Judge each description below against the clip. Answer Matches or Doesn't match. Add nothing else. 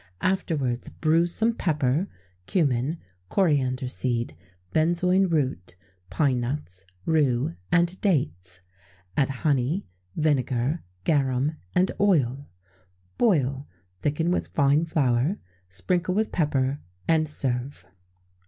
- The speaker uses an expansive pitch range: Doesn't match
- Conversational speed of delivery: Doesn't match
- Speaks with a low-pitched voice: Doesn't match